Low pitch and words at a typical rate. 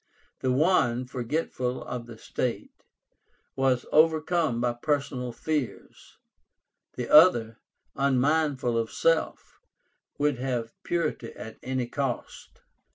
No: low, 130 Hz; slow, 100 wpm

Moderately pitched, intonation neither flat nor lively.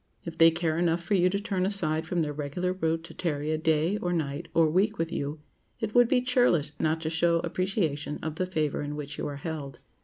Yes: medium, 165 Hz; average, 3.0 semitones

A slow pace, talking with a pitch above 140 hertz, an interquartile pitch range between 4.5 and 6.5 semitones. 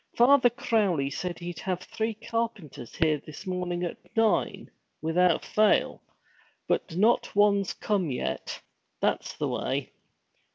Yes: slow, 125 wpm; medium, 185 Hz; average, 4.8 semitones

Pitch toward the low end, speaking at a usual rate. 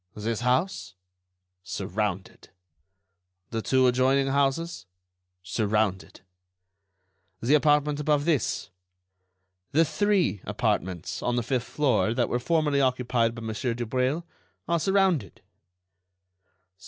No: low, 130 Hz; slow, 100 wpm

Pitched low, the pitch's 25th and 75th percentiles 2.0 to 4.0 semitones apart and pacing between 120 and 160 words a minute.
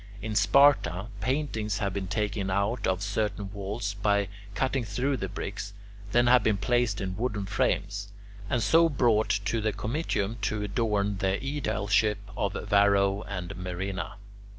Yes: low, 105 Hz; narrow, 2.5 semitones; average, 150 wpm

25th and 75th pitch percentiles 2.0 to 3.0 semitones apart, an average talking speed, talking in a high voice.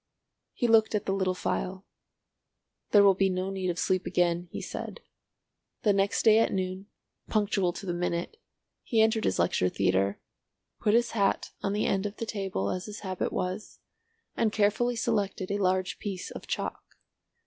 Yes: narrow, 2.5 semitones; average, 170 wpm; high, 195 Hz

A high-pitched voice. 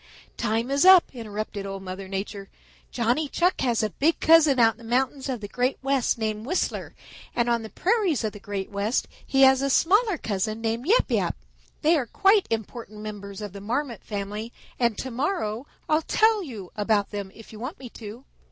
Yes: high, 235 Hz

